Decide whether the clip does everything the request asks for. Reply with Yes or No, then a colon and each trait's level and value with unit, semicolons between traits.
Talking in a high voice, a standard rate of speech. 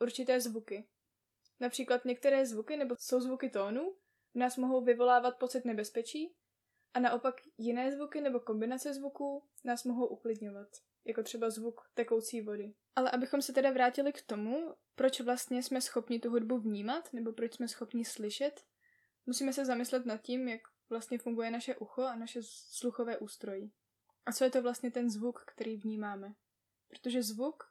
Yes: high, 245 Hz; average, 160 wpm